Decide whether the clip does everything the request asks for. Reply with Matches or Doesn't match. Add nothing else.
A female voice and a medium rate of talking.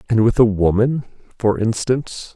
Doesn't match